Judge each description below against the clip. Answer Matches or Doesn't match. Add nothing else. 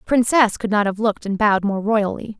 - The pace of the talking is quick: Matches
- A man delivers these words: Doesn't match